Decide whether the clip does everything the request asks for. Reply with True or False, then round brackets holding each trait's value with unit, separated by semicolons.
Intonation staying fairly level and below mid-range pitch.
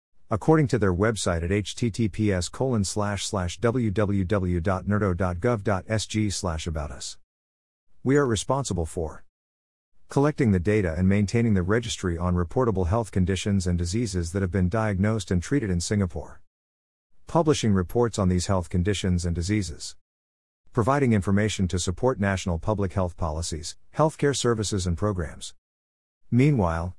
False (4.0 semitones; 95 Hz)